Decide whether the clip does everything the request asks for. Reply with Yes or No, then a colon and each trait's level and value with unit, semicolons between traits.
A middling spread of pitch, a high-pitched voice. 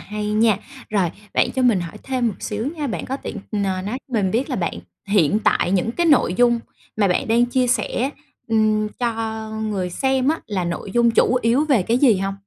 Yes: average, 3.4 semitones; high, 220 Hz